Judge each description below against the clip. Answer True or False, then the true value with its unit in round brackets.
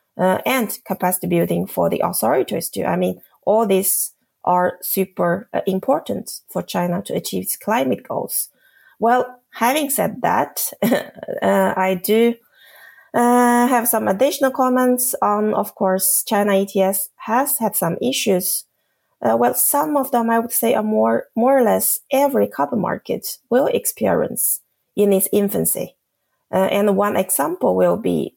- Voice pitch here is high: True (205 Hz)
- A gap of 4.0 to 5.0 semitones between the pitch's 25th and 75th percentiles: True (4.7 semitones)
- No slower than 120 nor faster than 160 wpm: True (150 wpm)